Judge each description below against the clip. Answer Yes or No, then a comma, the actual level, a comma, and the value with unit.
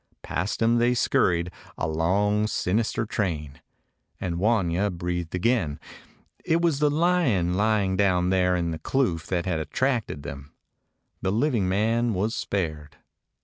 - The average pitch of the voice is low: Yes, very low, 95 Hz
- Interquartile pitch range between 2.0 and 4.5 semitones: No, average, 5.0 semitones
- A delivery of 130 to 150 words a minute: Yes, average, 140 wpm